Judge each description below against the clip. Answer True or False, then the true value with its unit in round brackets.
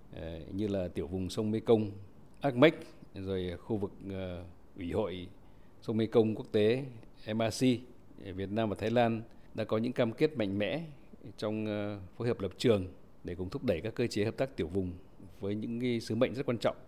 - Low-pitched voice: True (105 Hz)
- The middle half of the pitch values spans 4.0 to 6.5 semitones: False (3.6 semitones)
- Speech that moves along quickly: False (190 wpm)